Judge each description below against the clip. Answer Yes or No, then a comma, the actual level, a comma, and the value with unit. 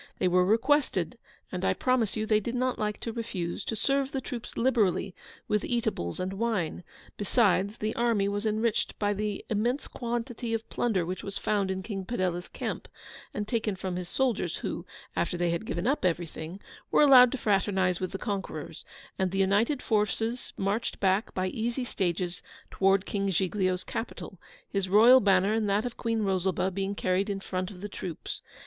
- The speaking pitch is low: No, high, 205 Hz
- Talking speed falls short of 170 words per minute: No, average, 180 wpm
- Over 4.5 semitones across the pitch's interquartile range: No, average, 3.5 semitones